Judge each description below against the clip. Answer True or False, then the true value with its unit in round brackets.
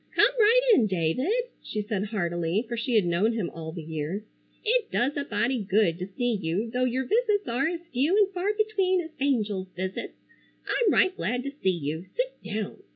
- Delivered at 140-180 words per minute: False (200 wpm)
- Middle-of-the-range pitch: False (230 Hz)